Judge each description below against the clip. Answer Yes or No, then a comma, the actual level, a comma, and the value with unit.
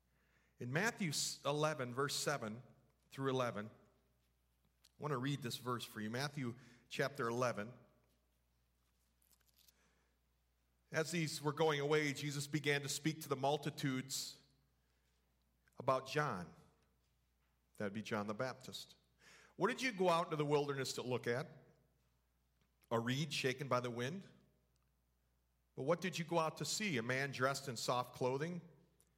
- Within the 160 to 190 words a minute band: No, average, 140 wpm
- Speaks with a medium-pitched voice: No, low, 125 Hz